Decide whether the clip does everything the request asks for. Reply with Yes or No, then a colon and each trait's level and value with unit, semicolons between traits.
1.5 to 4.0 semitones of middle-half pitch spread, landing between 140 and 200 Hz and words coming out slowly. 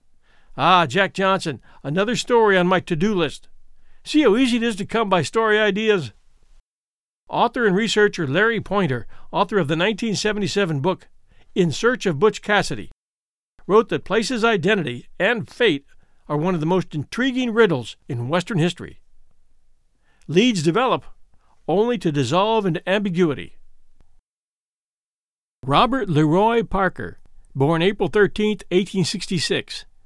No: average, 4.5 semitones; high, 190 Hz; slow, 130 wpm